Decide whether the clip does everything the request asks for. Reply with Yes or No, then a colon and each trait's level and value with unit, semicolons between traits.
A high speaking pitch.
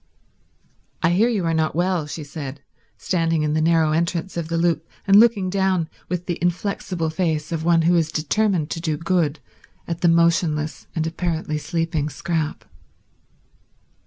No: medium, 165 Hz